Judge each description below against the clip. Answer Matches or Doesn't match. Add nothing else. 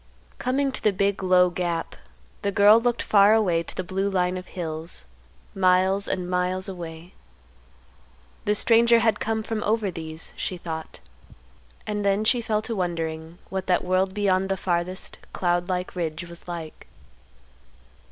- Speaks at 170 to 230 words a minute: Doesn't match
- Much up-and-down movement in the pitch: Doesn't match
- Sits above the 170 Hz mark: Matches